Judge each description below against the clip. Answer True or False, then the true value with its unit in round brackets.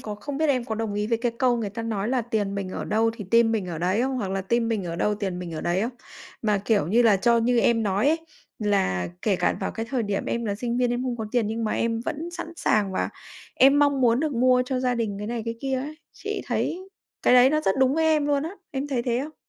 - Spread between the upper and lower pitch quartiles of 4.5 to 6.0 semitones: False (3.8 semitones)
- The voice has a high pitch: True (230 Hz)